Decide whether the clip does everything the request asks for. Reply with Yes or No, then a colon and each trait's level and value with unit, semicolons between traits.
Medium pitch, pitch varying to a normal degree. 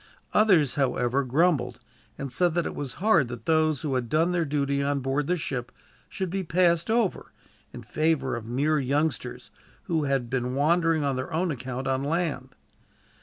Yes: medium, 145 Hz; average, 4.1 semitones